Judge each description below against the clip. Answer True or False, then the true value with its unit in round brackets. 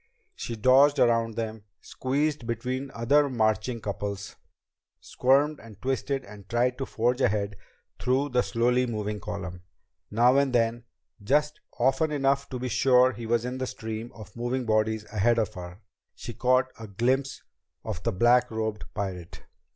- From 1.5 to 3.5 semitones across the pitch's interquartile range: True (3.1 semitones)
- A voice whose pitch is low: True (120 Hz)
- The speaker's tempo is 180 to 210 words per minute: False (160 wpm)